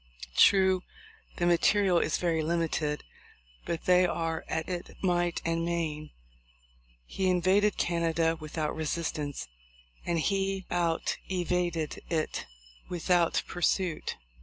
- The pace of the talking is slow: Yes, slow, 105 wpm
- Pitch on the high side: No, medium, 170 Hz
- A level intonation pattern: Yes, narrow, 1.9 semitones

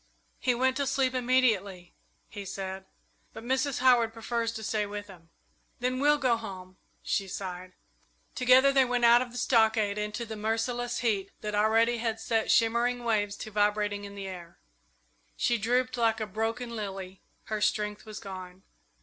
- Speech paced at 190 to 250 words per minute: No, average, 165 wpm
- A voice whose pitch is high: Yes, high, 225 Hz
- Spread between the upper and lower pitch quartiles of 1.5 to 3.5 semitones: Yes, average, 3.1 semitones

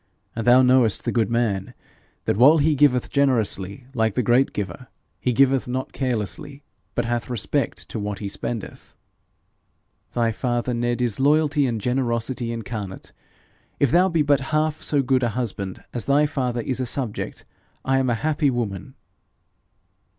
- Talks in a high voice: No, low, 125 Hz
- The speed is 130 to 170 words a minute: Yes, average, 160 wpm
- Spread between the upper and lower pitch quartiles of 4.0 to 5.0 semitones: No, average, 3.2 semitones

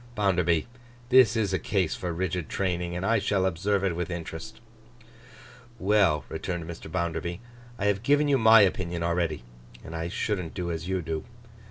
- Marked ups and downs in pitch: No, average, 3.3 semitones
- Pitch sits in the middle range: No, very low, 90 Hz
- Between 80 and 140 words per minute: No, average, 170 wpm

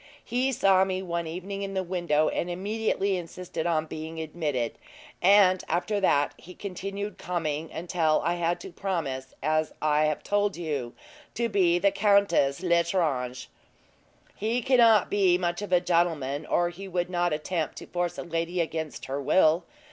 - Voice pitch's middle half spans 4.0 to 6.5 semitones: No, average, 3.4 semitones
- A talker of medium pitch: Yes, medium, 175 Hz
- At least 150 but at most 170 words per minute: Yes, average, 160 wpm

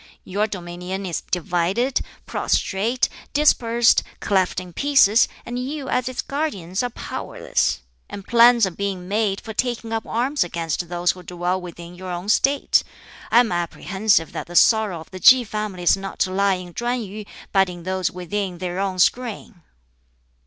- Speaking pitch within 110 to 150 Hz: No, high, 195 Hz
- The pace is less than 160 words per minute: No, average, 165 wpm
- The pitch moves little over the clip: No, average, 4.6 semitones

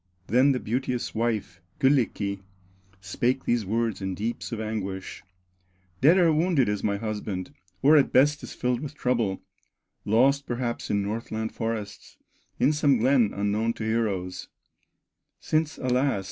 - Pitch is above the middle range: No, low, 115 Hz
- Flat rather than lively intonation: No, average, 4.3 semitones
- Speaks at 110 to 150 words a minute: Yes, average, 140 wpm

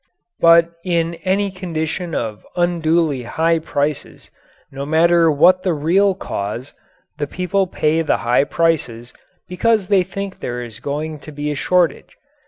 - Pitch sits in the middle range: Yes, medium, 165 Hz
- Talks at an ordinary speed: Yes, average, 145 wpm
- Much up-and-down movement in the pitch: No, average, 3.8 semitones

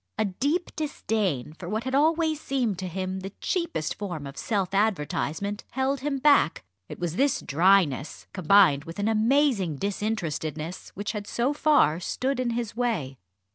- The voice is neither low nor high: No, high, 205 Hz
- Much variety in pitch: Yes, wide, 7.2 semitones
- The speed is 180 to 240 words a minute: No, average, 160 wpm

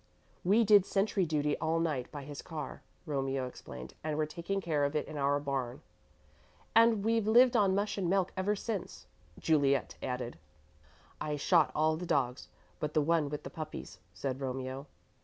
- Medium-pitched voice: Yes, medium, 155 Hz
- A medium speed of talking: Yes, average, 175 wpm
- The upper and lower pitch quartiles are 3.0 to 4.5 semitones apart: No, wide, 5.4 semitones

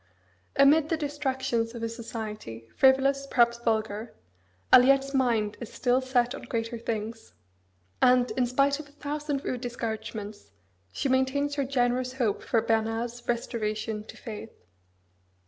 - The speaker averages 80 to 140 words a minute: Yes, slow, 135 wpm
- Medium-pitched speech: No, high, 245 Hz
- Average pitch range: Yes, average, 3.1 semitones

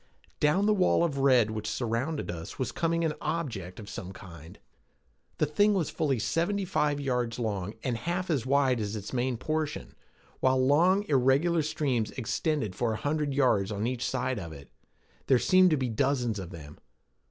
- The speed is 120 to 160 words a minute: No, average, 180 wpm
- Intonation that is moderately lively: No, wide, 5.9 semitones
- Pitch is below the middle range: Yes, low, 130 Hz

